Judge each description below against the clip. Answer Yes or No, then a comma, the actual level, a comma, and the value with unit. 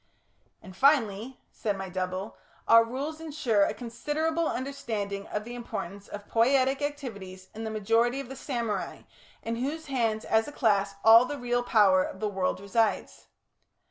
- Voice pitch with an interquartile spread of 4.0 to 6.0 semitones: Yes, average, 4.9 semitones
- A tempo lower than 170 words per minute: Yes, average, 160 wpm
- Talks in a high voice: Yes, high, 230 Hz